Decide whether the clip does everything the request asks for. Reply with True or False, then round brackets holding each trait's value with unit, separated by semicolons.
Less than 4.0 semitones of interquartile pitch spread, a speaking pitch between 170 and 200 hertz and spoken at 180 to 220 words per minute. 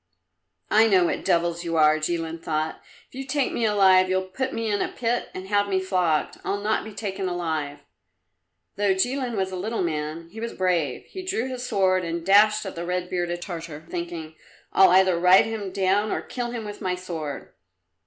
True (3.6 semitones; 185 Hz; 200 wpm)